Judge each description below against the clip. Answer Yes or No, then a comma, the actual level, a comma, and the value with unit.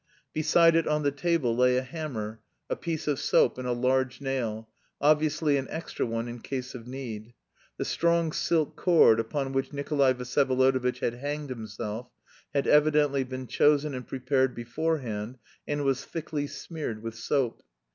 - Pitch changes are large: No, average, 3.4 semitones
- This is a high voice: No, low, 135 Hz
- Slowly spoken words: No, average, 160 wpm